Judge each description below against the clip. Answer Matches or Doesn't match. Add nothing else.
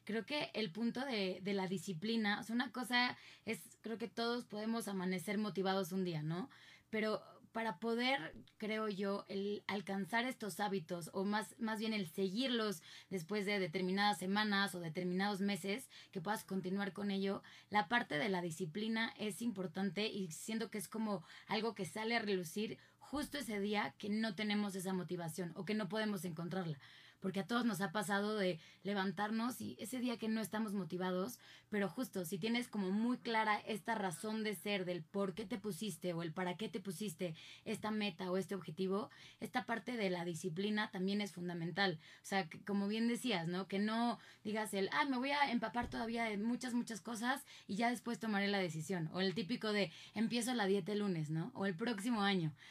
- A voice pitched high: Matches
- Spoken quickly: Matches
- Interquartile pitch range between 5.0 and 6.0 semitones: Doesn't match